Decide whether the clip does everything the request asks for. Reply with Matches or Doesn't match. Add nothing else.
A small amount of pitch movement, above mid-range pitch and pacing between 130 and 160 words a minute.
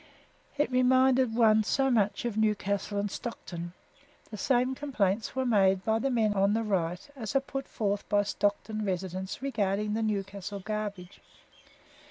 Doesn't match